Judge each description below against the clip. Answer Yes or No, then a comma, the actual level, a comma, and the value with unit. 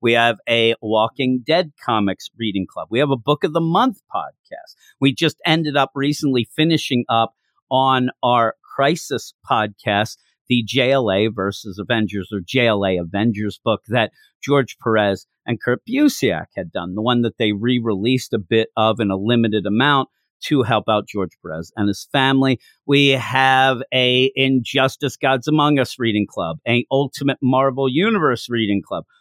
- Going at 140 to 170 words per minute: Yes, average, 160 wpm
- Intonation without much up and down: No, average, 3.7 semitones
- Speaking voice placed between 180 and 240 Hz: No, low, 125 Hz